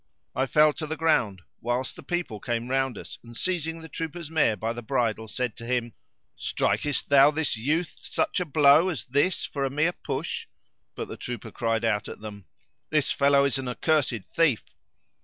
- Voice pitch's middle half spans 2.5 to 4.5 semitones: No, average, 4.9 semitones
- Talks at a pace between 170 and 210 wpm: Yes, average, 190 wpm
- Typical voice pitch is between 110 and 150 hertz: Yes, low, 135 Hz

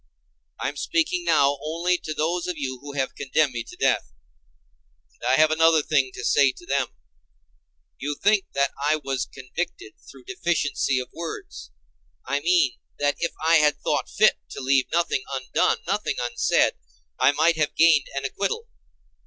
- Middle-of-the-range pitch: Yes, medium, 145 Hz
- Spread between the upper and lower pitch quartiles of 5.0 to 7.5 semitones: No, average, 4.0 semitones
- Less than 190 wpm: Yes, average, 165 wpm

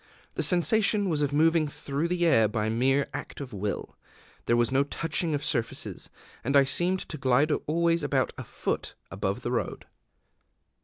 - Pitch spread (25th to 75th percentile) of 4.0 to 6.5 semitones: Yes, wide, 5.4 semitones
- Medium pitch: Yes, medium, 145 Hz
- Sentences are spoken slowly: No, average, 170 wpm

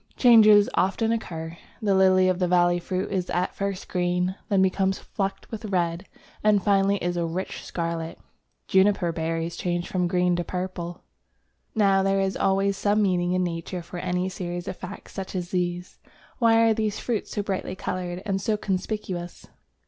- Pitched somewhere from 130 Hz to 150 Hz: No, medium, 185 Hz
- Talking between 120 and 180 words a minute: Yes, average, 170 wpm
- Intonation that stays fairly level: Yes, narrow, 2.1 semitones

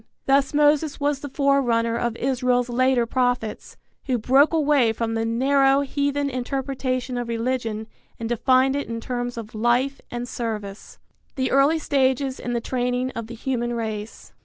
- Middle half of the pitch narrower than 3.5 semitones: Yes, average, 2.8 semitones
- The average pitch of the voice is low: No, very high, 250 Hz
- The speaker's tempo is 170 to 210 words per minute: No, average, 160 wpm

